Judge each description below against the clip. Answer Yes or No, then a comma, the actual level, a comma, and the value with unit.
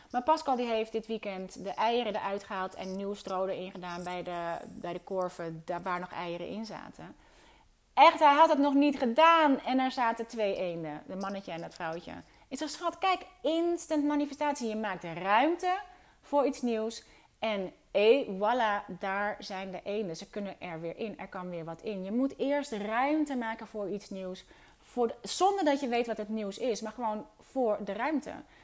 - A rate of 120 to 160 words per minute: No, average, 195 wpm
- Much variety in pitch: Yes, wide, 6.2 semitones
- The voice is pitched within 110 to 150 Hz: No, high, 220 Hz